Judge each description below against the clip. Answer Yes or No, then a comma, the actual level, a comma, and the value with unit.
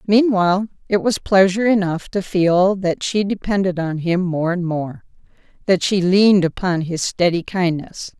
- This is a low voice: No, medium, 185 Hz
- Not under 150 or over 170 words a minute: Yes, average, 160 wpm